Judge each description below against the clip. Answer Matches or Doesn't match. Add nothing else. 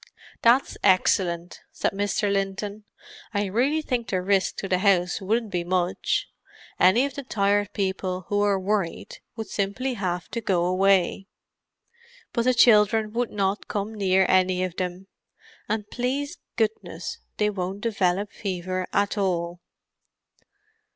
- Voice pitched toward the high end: Matches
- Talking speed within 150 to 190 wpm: Doesn't match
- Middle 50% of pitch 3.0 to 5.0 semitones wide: Doesn't match